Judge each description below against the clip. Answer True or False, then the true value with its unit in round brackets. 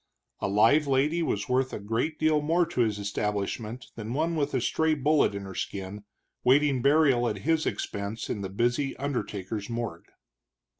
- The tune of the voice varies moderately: False (6.1 semitones)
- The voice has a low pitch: True (125 Hz)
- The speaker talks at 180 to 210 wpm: False (170 wpm)